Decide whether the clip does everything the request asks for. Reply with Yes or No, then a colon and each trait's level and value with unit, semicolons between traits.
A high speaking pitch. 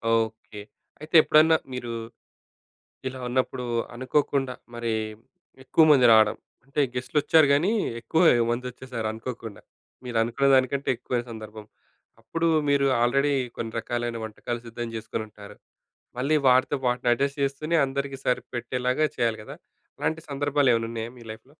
No: low, 125 Hz